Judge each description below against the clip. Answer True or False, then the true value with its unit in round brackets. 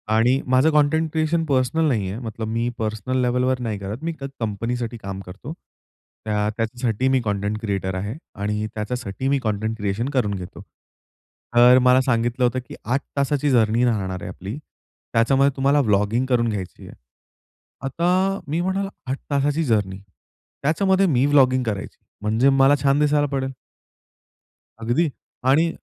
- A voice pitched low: True (125 Hz)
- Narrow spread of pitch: False (4.6 semitones)